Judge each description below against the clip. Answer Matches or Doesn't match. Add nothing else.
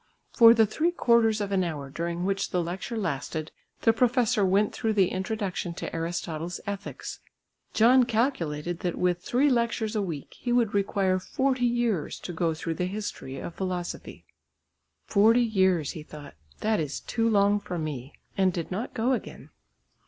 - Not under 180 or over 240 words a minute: Doesn't match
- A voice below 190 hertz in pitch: Doesn't match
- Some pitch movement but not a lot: Matches